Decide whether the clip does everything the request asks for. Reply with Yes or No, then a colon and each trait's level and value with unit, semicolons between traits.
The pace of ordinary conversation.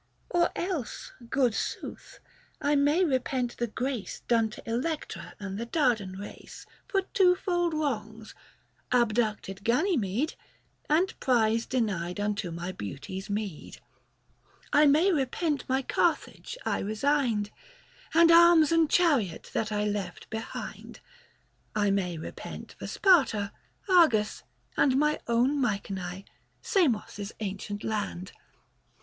No: slow, 125 wpm